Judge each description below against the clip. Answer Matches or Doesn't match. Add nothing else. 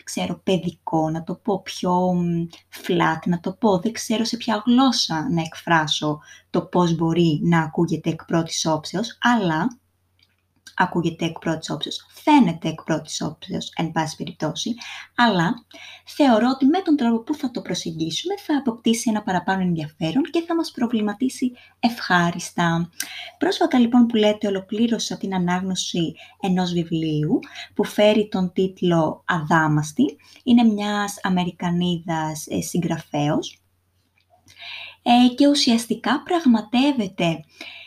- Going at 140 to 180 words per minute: Doesn't match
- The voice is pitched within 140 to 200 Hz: Matches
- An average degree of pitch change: Doesn't match